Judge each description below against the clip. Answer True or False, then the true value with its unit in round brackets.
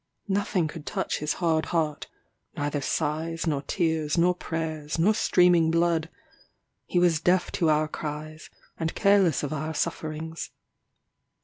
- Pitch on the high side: False (160 Hz)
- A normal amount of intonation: False (2.1 semitones)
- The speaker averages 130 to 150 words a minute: True (135 wpm)